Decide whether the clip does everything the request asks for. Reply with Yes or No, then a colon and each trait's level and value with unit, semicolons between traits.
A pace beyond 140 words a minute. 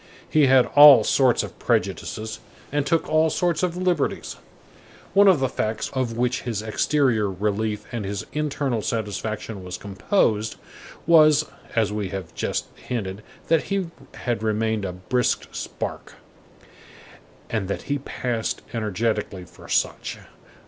No: slow, 135 wpm